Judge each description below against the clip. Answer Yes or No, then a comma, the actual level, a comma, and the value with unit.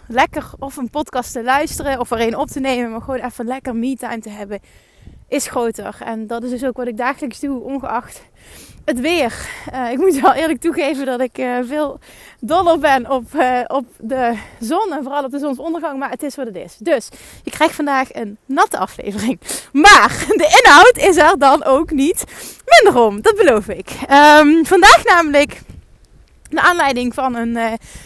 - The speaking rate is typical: Yes, average, 190 wpm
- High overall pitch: Yes, very high, 270 Hz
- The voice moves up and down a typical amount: Yes, average, 3.6 semitones